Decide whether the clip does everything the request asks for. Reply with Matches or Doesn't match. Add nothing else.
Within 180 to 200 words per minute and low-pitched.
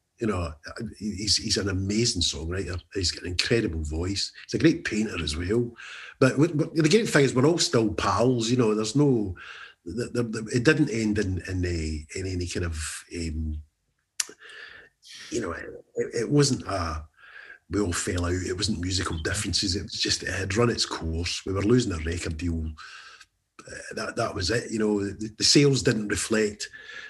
Matches